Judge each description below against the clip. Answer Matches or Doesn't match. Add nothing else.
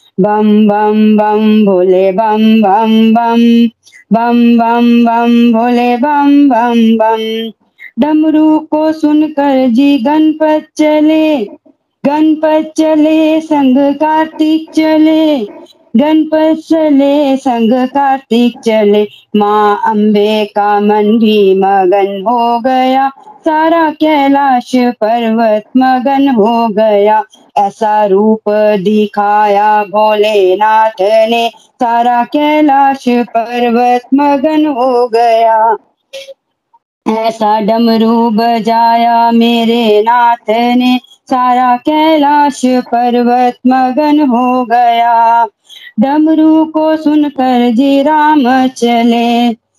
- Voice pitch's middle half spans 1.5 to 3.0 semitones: Doesn't match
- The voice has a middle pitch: Doesn't match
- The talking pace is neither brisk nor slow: Doesn't match